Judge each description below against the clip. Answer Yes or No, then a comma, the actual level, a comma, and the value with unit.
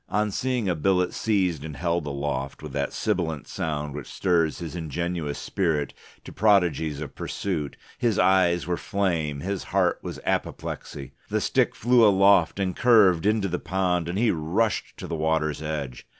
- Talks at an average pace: Yes, average, 165 wpm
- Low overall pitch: Yes, very low, 85 Hz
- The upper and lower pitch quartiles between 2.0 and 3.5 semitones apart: No, average, 4.1 semitones